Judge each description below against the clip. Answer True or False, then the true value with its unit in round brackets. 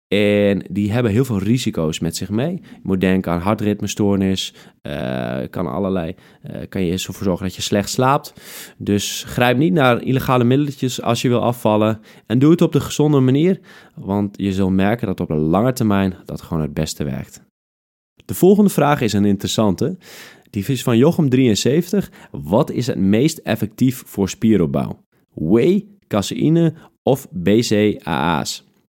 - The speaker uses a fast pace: False (160 wpm)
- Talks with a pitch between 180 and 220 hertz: False (105 Hz)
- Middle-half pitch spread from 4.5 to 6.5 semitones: True (5.4 semitones)